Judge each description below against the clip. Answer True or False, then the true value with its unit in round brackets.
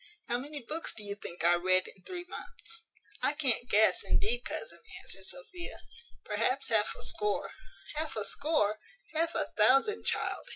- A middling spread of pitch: False (7.9 semitones)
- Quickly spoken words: False (165 wpm)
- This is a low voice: False (260 Hz)